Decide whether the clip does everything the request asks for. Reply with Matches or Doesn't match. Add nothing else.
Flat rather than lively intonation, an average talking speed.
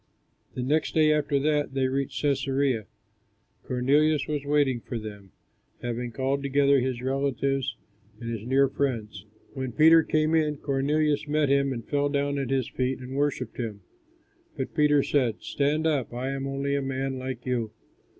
Matches